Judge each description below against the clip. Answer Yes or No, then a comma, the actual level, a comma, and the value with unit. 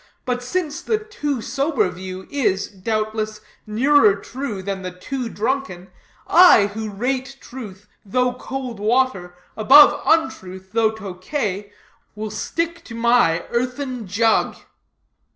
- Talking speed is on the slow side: Yes, slow, 120 wpm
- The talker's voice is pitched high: Yes, high, 225 Hz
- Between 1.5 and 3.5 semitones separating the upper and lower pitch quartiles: No, average, 5.1 semitones